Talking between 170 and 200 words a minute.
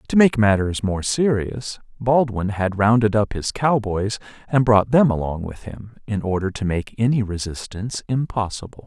No: average, 160 wpm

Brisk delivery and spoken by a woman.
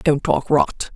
No: average, 190 wpm; female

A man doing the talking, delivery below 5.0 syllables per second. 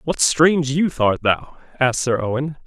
No: male; 5.1 syllables/s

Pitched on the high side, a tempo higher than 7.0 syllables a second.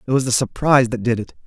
No: low, 125 Hz; 7.2 syllables/s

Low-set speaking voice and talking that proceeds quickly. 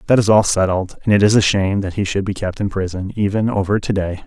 Yes: low, 100 Hz; fast, 280 wpm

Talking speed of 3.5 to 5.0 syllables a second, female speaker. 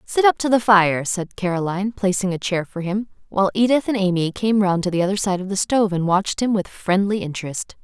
No: 5.9 syllables/s; female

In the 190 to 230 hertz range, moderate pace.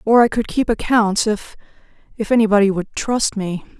Yes: high, 215 Hz; average, 160 wpm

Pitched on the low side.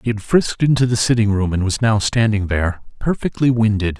Yes: low, 110 Hz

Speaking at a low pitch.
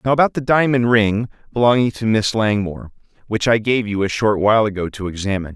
Yes: low, 110 Hz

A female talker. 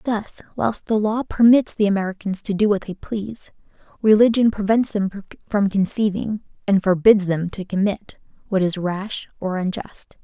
Yes: female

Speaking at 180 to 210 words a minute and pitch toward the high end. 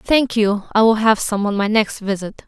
No: fast, 240 wpm; high, 215 Hz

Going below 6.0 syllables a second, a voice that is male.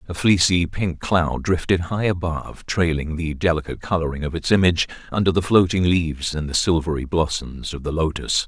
Yes: 5.5 syllables/s; male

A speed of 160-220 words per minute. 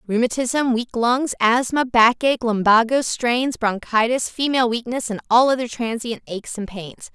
No: average, 145 wpm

